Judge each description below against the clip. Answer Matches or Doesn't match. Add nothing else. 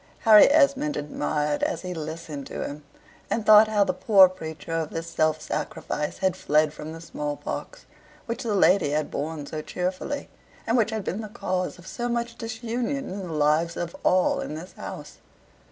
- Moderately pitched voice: Matches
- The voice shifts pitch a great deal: Matches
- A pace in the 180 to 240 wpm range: Matches